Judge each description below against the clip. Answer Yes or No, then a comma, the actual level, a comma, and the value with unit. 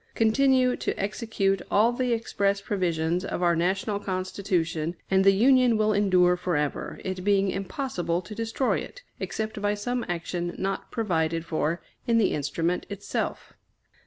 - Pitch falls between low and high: No, high, 195 Hz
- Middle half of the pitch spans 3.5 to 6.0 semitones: Yes, average, 3.9 semitones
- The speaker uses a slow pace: No, average, 145 wpm